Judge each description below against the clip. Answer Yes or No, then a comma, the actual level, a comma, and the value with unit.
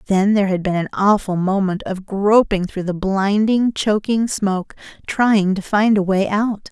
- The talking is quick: No, average, 180 wpm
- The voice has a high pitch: Yes, high, 200 Hz